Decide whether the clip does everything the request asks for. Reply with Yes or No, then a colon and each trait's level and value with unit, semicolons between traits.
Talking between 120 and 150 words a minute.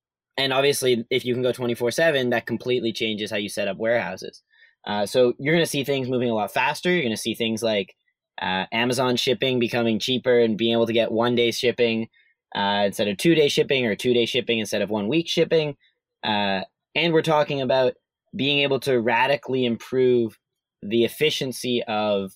No: average, 200 wpm